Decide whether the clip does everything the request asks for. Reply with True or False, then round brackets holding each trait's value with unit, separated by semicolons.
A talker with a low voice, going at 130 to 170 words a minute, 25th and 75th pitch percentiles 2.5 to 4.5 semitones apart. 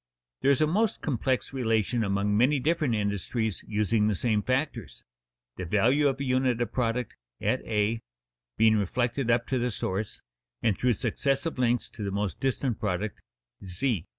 True (115 Hz; 165 wpm; 3.9 semitones)